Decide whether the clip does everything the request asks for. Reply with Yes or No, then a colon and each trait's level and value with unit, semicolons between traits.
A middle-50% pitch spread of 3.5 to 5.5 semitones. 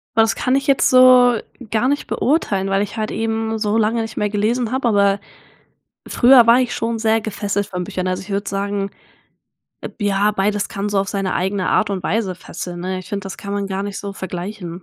No: narrow, 2.5 semitones